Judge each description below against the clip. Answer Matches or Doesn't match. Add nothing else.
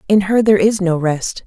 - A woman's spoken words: Matches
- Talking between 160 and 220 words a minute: Doesn't match